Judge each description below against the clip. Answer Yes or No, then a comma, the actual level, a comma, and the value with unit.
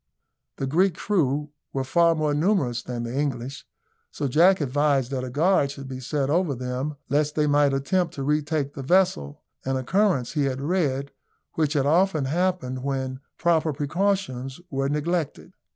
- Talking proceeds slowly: No, average, 165 wpm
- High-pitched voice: No, medium, 145 Hz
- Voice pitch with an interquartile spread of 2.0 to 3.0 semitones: No, average, 3.8 semitones